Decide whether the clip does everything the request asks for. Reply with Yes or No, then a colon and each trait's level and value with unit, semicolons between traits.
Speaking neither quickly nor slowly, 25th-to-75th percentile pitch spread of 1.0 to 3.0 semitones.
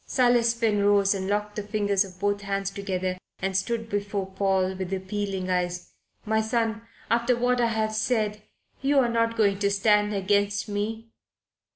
Yes: average, 170 wpm; narrow, 2.5 semitones